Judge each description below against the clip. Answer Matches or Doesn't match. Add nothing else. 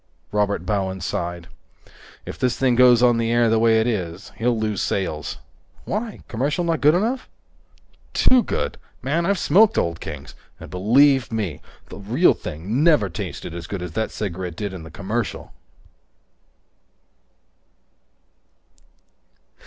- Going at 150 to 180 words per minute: Doesn't match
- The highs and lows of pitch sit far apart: Matches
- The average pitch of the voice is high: Doesn't match